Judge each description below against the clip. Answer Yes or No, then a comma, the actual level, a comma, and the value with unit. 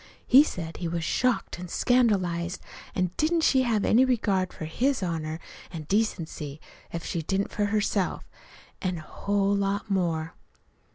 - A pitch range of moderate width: Yes, average, 4.5 semitones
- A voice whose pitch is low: No, high, 190 Hz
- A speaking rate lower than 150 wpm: No, average, 160 wpm